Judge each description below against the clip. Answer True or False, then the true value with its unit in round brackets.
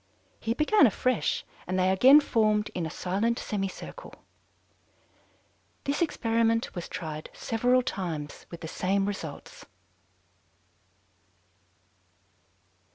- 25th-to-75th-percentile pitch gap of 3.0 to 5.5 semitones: True (5.0 semitones)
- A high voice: True (210 Hz)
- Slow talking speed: True (95 wpm)